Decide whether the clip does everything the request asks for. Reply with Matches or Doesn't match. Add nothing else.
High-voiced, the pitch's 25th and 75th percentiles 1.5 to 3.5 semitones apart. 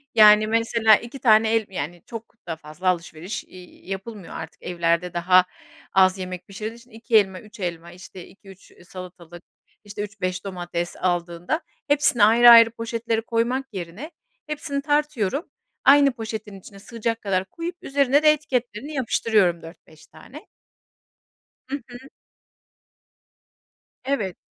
Doesn't match